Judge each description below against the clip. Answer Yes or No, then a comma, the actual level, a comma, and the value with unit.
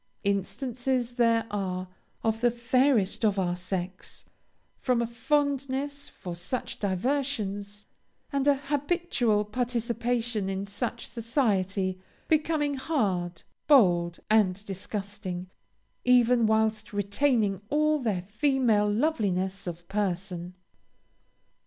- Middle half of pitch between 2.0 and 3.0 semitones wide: No, average, 5.0 semitones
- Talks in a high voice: Yes, high, 220 Hz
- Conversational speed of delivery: No, slow, 100 wpm